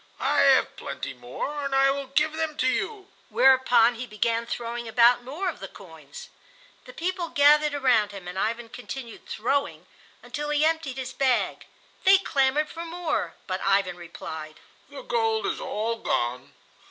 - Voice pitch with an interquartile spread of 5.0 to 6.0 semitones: Yes, wide, 5.6 semitones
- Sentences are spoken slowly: No, average, 165 wpm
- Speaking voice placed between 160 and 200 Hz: No, very high, 265 Hz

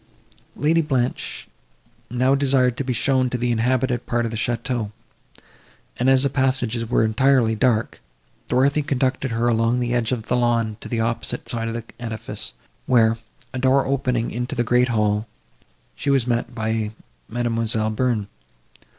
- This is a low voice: Yes, low, 120 Hz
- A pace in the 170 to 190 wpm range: No, average, 160 wpm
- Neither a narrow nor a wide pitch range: No, narrow, 2.3 semitones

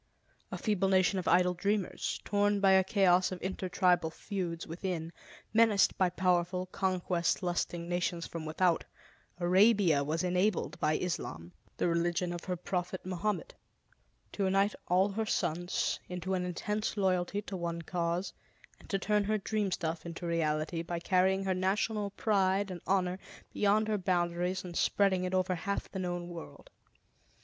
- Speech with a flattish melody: Yes, narrow, 2.2 semitones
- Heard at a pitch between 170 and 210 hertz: Yes, medium, 185 Hz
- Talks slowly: No, average, 155 wpm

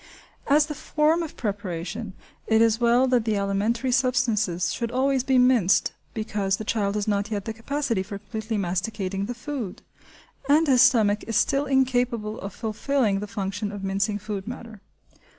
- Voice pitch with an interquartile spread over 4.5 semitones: No, average, 3.9 semitones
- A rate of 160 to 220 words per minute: Yes, average, 170 wpm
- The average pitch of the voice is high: Yes, high, 220 Hz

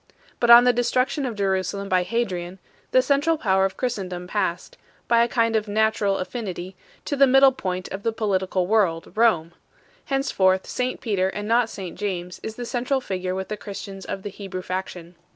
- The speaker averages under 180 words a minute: No, average, 190 wpm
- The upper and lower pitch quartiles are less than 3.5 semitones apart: No, average, 4.2 semitones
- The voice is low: No, high, 205 Hz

